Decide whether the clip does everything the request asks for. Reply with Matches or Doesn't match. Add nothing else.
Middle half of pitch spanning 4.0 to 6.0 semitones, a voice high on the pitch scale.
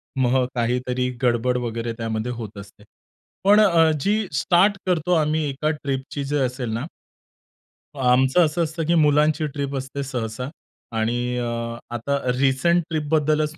Doesn't match